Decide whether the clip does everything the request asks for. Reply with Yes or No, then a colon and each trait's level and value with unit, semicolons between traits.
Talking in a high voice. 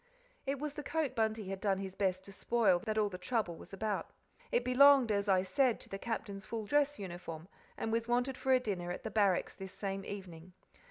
Yes: high, 210 Hz